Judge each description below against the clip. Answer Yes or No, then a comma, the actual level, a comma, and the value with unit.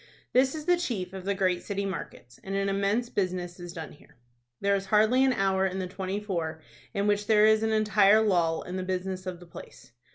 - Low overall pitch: No, high, 195 Hz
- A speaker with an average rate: No, fast, 225 wpm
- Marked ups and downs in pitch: No, narrow, 2.5 semitones